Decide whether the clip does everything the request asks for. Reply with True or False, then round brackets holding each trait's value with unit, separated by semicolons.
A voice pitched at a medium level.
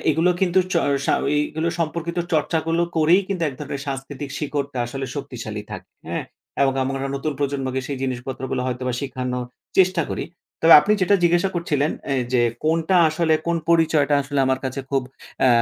True (145 Hz)